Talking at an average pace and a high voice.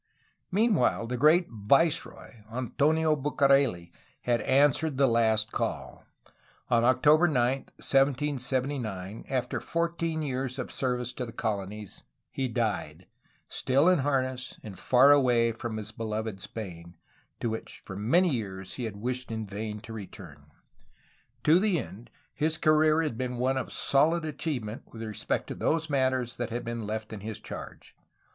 No: average, 150 wpm; low, 125 Hz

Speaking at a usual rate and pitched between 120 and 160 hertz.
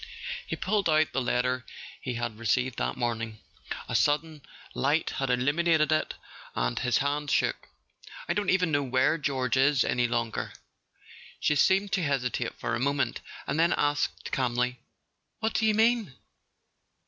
Yes: average, 160 wpm; medium, 140 Hz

